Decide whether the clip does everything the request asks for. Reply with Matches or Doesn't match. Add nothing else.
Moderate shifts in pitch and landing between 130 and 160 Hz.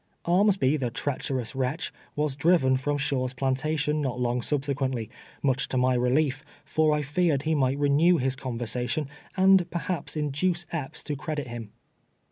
Matches